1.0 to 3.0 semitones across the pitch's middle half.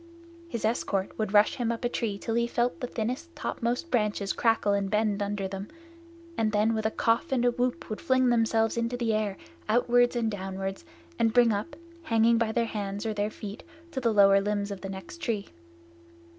Yes: average, 2.7 semitones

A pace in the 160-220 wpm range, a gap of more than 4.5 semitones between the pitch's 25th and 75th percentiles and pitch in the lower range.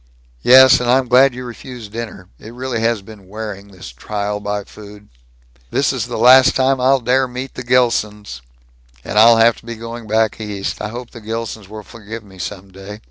No: average, 200 wpm; average, 3.1 semitones; low, 110 Hz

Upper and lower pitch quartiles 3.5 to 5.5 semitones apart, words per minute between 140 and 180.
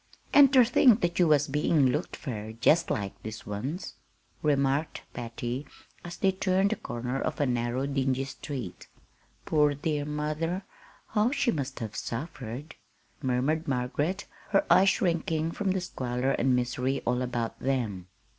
Yes: average, 5.1 semitones; average, 150 wpm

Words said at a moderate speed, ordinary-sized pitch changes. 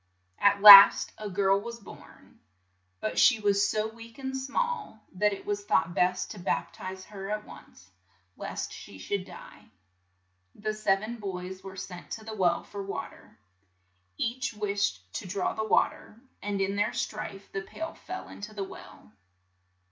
No: average, 170 wpm; narrow, 2.3 semitones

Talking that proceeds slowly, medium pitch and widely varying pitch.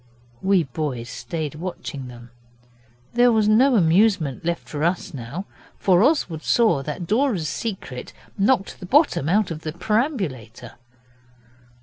Yes: slow, 130 wpm; medium, 175 Hz; wide, 6.5 semitones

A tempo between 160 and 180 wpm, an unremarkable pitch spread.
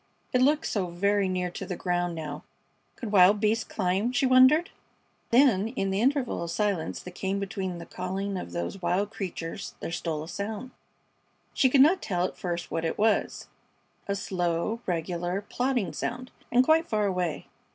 Yes: average, 175 wpm; average, 4.6 semitones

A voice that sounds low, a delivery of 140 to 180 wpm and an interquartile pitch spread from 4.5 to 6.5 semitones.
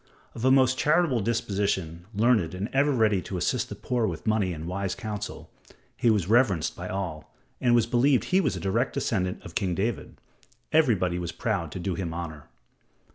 No: low, 105 Hz; average, 190 wpm; average, 5.1 semitones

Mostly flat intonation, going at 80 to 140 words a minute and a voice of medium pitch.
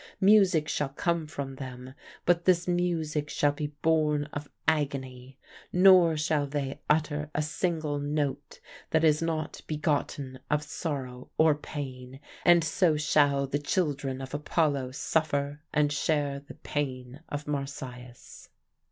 Yes: narrow, 2.2 semitones; slow, 135 wpm; medium, 145 Hz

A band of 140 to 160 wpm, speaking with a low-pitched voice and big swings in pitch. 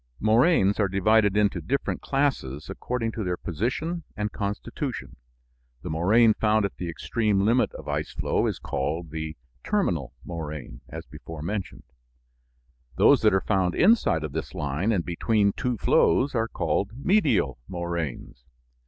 Yes: average, 145 wpm; low, 100 Hz; wide, 5.9 semitones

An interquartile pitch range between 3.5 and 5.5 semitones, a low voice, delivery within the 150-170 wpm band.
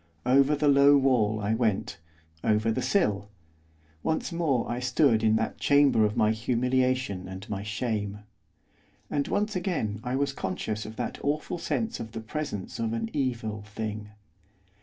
Yes: average, 4.6 semitones; low, 115 Hz; average, 160 wpm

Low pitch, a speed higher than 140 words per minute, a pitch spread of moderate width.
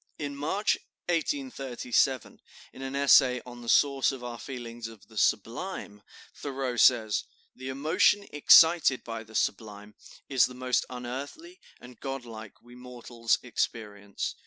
No: low, 125 Hz; slow, 135 wpm; average, 3.1 semitones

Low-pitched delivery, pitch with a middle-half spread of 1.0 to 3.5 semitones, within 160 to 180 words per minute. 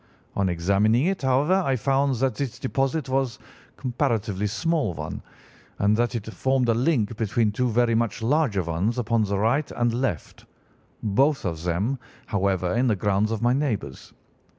No: low, 115 Hz; average, 4.7 semitones; average, 165 wpm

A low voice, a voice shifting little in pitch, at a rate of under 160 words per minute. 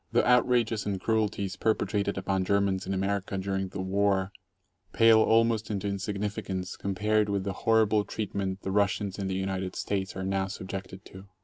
No: low, 100 Hz; narrow, 1.7 semitones; average, 170 wpm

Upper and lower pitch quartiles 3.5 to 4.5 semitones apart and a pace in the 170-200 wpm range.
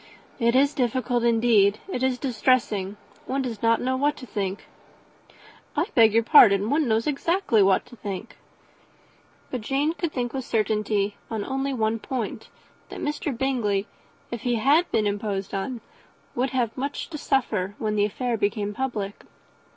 No: average, 4.1 semitones; average, 160 wpm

